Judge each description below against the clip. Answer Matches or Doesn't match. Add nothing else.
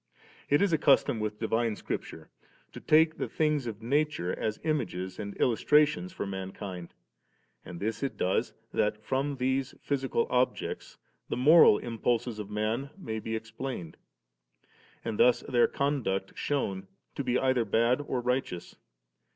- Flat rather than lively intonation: Doesn't match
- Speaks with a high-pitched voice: Doesn't match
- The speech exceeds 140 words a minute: Matches